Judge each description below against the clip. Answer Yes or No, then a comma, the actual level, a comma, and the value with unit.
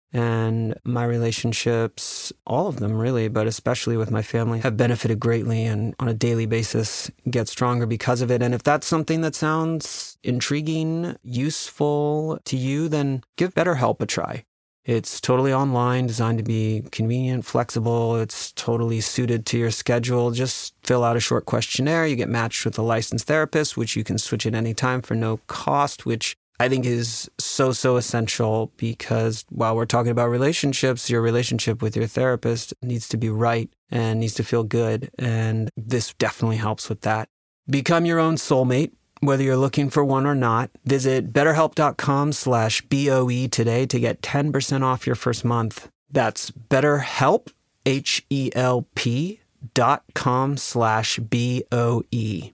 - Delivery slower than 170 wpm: Yes, average, 160 wpm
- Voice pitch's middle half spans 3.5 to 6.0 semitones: No, average, 2.9 semitones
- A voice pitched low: Yes, low, 120 Hz